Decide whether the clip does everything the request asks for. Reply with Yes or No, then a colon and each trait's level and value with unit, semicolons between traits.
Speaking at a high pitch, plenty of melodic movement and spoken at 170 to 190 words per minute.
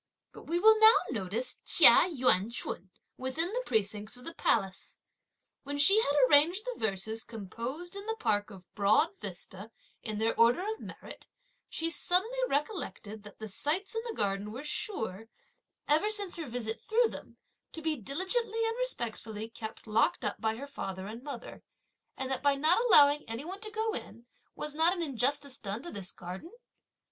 Yes: very high, 270 Hz; wide, 8.3 semitones; average, 175 wpm